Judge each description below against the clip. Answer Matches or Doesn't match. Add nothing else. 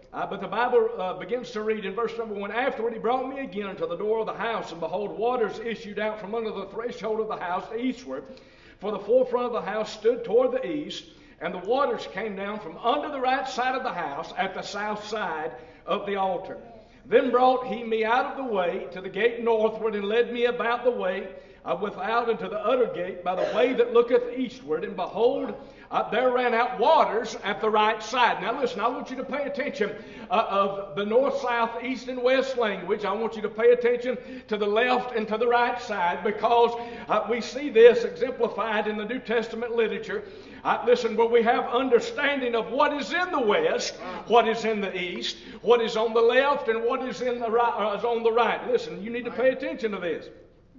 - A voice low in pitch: Doesn't match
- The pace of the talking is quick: Matches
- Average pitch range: Matches